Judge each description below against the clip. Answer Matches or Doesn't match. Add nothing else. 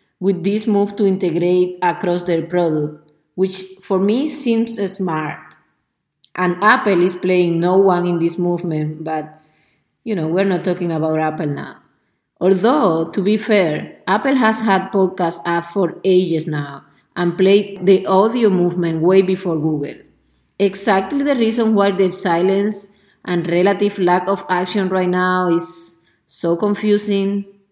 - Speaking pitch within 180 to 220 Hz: Matches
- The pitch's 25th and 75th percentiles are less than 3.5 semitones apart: Matches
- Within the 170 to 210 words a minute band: Doesn't match